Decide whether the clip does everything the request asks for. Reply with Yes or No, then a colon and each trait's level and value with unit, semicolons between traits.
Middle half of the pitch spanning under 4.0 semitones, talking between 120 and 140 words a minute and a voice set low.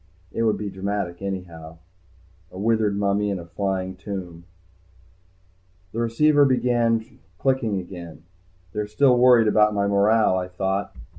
Yes: average, 3.4 semitones; slow, 135 wpm; low, 100 Hz